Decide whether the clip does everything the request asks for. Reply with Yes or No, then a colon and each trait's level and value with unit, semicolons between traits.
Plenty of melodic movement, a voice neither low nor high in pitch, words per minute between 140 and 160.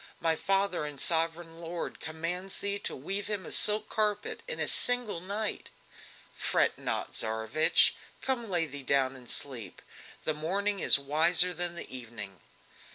Yes: wide, 5.8 semitones; medium, 170 Hz; average, 155 wpm